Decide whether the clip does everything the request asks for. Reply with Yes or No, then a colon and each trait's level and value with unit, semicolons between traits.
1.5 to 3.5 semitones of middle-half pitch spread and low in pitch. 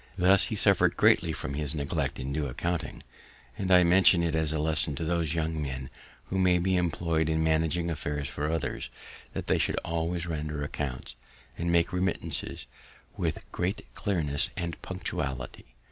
Yes: average, 2.8 semitones; very low, 80 Hz